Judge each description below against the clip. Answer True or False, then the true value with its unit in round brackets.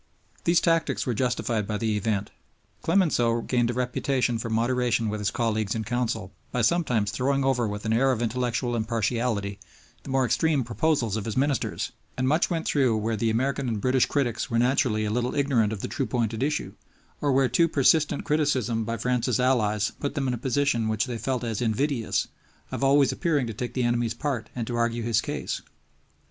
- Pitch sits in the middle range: False (120 Hz)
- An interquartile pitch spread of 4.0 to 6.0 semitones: False (3.1 semitones)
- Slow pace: False (200 wpm)